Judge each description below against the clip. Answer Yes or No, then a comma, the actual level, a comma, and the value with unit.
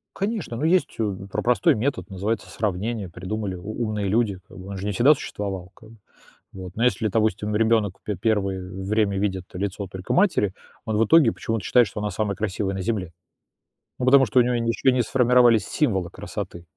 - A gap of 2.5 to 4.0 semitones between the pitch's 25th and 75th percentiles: Yes, average, 3.5 semitones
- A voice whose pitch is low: Yes, low, 105 Hz